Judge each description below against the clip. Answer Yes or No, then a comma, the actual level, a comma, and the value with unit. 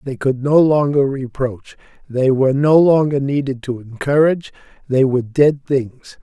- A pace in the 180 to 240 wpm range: No, average, 155 wpm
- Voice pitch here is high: No, low, 135 Hz